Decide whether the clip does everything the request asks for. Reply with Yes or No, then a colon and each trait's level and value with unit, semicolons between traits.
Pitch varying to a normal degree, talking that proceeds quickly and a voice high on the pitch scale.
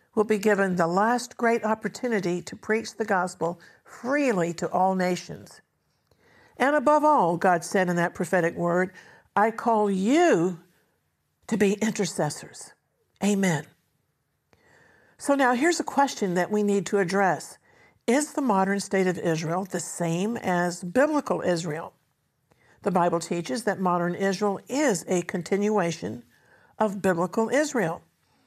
No: average, 4.2 semitones; slow, 135 wpm; high, 195 Hz